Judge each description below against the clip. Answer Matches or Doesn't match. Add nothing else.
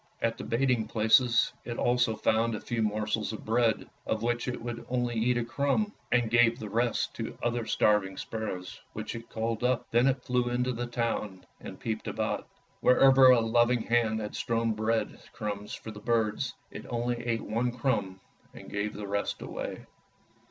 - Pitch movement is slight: Matches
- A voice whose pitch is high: Doesn't match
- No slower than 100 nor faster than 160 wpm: Doesn't match